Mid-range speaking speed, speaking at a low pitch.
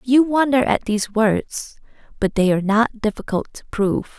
No: average, 170 wpm; high, 225 Hz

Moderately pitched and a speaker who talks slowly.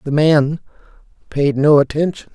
Yes: medium, 150 Hz; slow, 130 wpm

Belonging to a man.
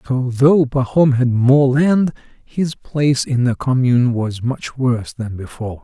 Yes: male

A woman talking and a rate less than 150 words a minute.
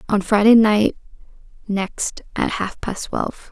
Yes: female; slow, 135 wpm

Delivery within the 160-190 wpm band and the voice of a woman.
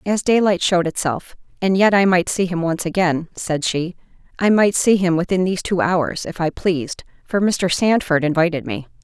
Yes: average, 185 wpm; female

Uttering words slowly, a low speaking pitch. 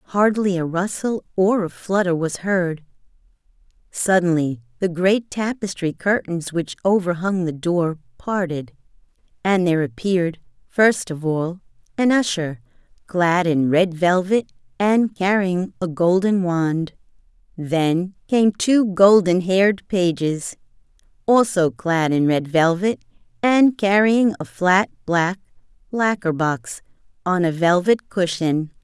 No: slow, 120 wpm; medium, 180 Hz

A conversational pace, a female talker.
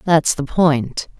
Yes: average, 150 wpm; female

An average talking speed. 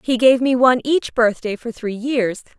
No: fast, 210 wpm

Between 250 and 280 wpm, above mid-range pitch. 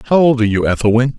No: fast, 255 wpm; low, 120 Hz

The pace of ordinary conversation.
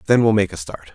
No: fast, 315 wpm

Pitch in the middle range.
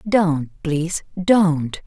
Yes: medium, 170 Hz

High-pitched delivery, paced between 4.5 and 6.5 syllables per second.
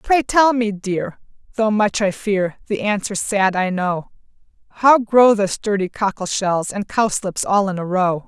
No: high, 205 Hz; 4.2 syllables/s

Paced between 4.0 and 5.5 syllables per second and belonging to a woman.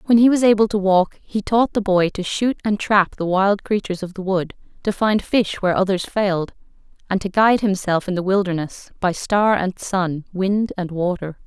Yes: 5.0 syllables/s; female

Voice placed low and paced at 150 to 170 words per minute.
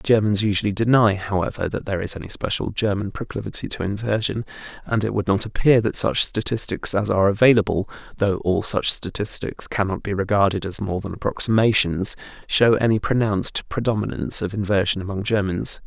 Yes: low, 105 Hz; average, 165 wpm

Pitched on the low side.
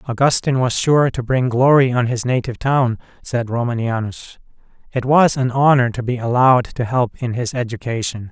Yes: low, 125 Hz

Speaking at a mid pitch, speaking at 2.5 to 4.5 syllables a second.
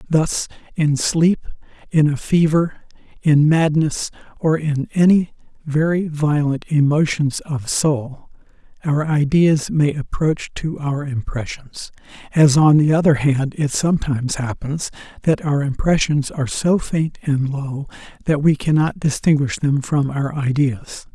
Yes: medium, 150 Hz; 4.0 syllables/s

